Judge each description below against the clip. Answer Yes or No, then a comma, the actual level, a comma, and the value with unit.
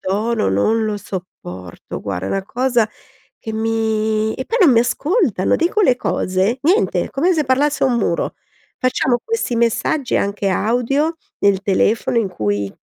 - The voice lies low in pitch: No, high, 225 Hz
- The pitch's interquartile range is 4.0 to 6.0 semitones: Yes, average, 5.0 semitones